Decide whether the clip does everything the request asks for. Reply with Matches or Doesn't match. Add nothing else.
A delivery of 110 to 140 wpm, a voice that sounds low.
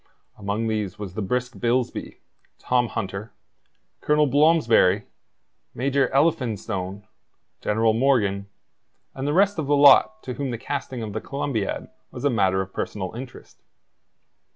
Matches